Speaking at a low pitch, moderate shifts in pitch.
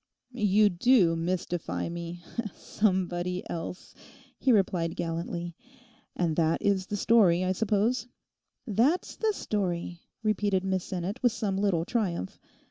No: high, 190 Hz; average, 3.6 semitones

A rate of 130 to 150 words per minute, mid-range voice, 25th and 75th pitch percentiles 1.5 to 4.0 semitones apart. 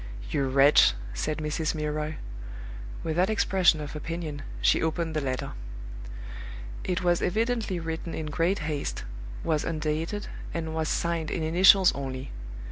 Yes: slow, 135 wpm; medium, 160 Hz; narrow, 2.4 semitones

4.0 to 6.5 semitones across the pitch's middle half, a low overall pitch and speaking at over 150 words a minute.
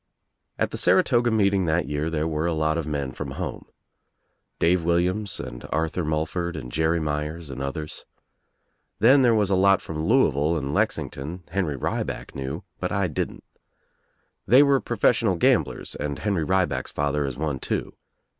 Yes: average, 4.7 semitones; very low, 80 Hz; average, 165 wpm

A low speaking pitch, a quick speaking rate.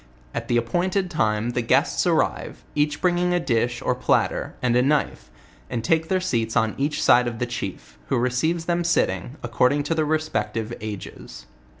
No: low, 125 Hz; average, 180 wpm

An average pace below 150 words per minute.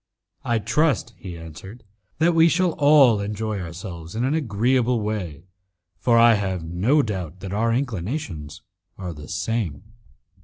Yes: average, 140 wpm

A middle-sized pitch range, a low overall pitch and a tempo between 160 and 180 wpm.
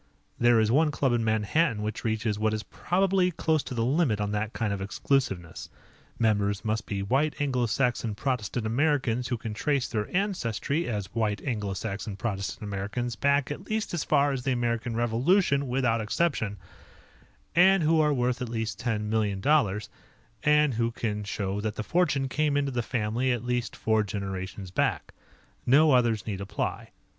Yes: average, 4.9 semitones; low, 115 Hz; average, 170 wpm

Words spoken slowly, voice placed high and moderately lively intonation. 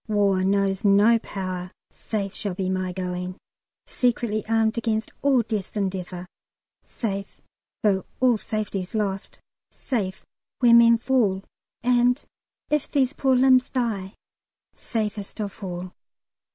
Yes: slow, 120 wpm; high, 210 Hz; average, 3.6 semitones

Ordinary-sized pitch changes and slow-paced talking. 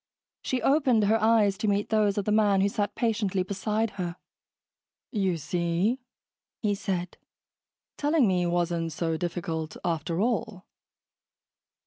Yes: average, 3.8 semitones; slow, 130 wpm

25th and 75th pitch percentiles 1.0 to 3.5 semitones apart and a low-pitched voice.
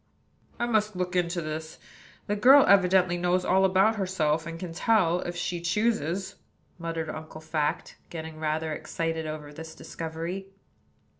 No: average, 3.0 semitones; medium, 175 Hz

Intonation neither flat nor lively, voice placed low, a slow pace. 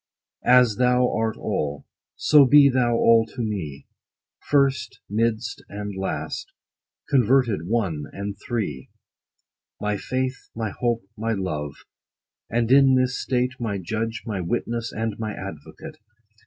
Yes: average, 3.7 semitones; low, 115 Hz; slow, 130 wpm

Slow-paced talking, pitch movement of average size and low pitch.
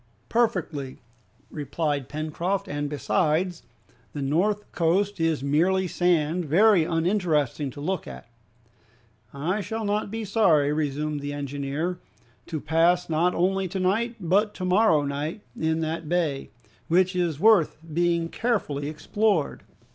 No: slow, 125 wpm; average, 4.3 semitones; medium, 165 Hz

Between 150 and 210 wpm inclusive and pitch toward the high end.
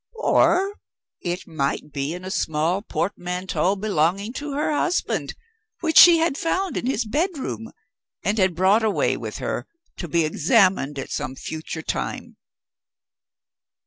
No: average, 140 wpm; high, 195 Hz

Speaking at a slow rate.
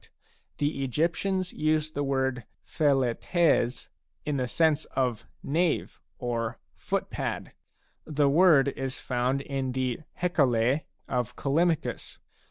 Yes: slow, 130 wpm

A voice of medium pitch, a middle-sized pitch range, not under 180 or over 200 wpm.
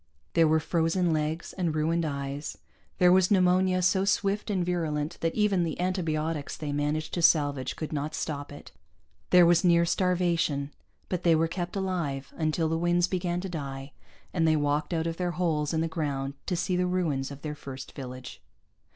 Yes: medium, 165 Hz; average, 3.2 semitones; average, 185 wpm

